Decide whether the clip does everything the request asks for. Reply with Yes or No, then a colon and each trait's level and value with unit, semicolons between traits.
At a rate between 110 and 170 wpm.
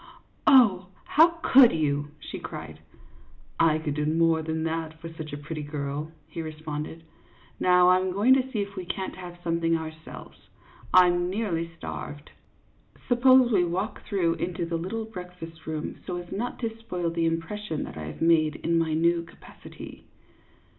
No: average, 180 wpm